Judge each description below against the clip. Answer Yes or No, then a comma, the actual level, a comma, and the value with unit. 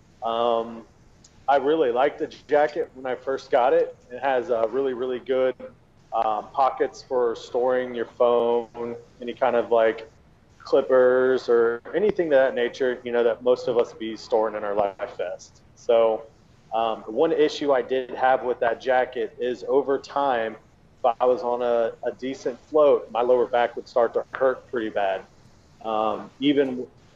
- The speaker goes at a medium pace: Yes, average, 170 wpm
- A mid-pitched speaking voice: No, low, 125 Hz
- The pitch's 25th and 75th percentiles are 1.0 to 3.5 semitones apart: Yes, average, 2.8 semitones